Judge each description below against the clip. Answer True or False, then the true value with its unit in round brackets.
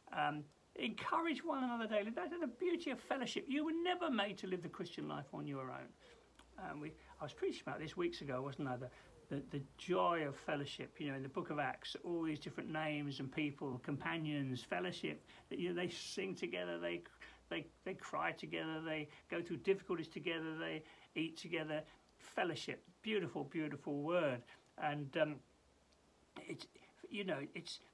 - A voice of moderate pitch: True (155 Hz)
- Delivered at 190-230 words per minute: False (180 wpm)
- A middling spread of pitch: True (4.2 semitones)